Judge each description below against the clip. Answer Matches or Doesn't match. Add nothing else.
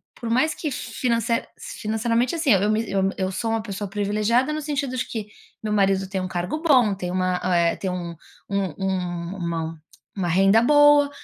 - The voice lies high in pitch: Matches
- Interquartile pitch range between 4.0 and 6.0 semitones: Matches